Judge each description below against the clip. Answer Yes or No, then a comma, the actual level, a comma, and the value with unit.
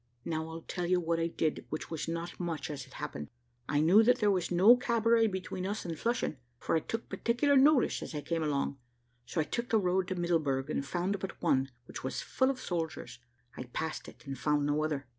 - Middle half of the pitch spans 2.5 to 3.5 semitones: No, average, 5.3 semitones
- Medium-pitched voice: Yes, medium, 170 Hz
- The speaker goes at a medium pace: No, fast, 225 wpm